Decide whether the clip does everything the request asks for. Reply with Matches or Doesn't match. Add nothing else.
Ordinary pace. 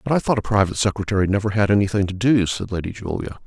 Doesn't match